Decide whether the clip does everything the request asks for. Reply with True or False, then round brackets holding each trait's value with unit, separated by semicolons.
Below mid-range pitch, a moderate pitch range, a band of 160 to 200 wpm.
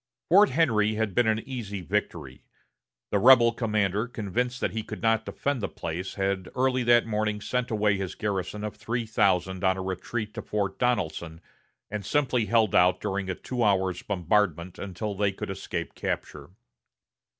True (105 Hz; 3.4 semitones; 170 wpm)